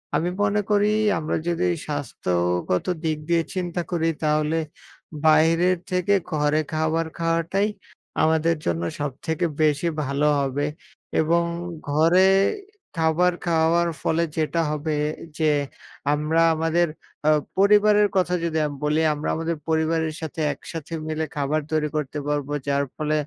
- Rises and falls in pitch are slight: Yes, narrow, 2.1 semitones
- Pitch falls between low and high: Yes, medium, 160 Hz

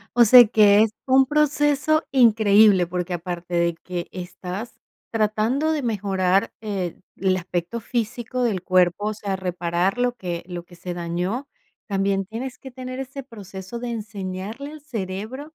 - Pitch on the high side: Yes, high, 205 Hz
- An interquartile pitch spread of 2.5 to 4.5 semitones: No, average, 5.1 semitones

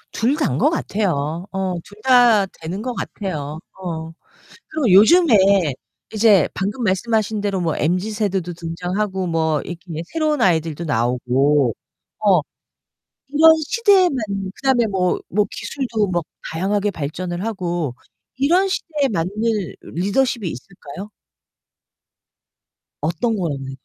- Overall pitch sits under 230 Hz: Yes, high, 190 Hz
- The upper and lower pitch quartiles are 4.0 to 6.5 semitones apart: Yes, wide, 5.4 semitones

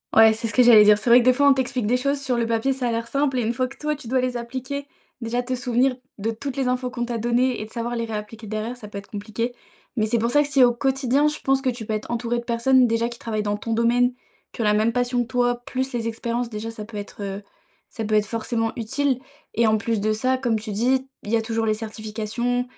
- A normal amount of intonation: No, narrow, 2.3 semitones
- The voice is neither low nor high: No, high, 235 Hz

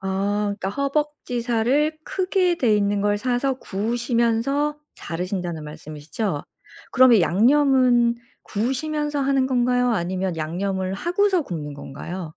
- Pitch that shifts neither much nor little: No, wide, 6.3 semitones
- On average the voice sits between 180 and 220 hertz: No, high, 235 Hz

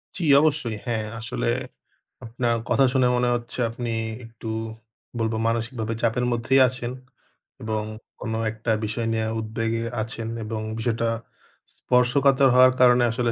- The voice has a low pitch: Yes, low, 115 Hz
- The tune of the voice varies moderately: No, narrow, 1.8 semitones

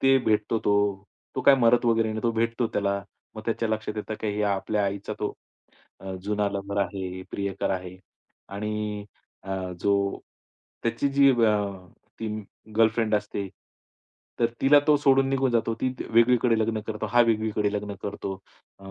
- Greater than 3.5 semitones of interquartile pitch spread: No, narrow, 2.4 semitones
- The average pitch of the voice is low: Yes, low, 110 Hz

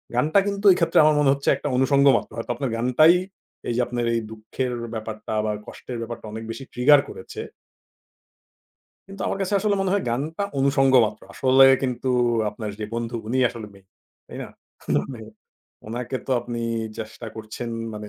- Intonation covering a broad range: No, average, 3.8 semitones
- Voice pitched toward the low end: Yes, low, 125 Hz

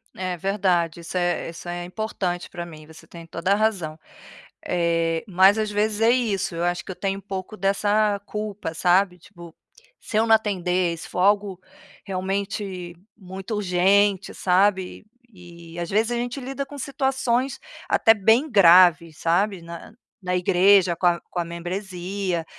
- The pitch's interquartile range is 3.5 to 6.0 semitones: No, average, 3.0 semitones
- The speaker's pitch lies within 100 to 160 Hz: No, high, 190 Hz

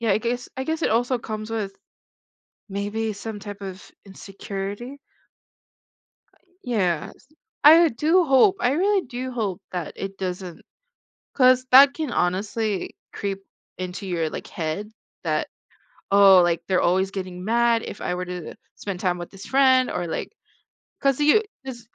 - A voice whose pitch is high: Yes, high, 210 Hz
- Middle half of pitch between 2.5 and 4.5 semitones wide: No, average, 5.2 semitones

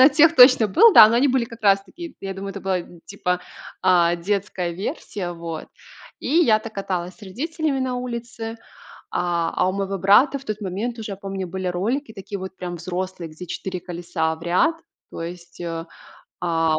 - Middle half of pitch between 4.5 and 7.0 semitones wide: Yes, average, 4.8 semitones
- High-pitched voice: Yes, high, 195 Hz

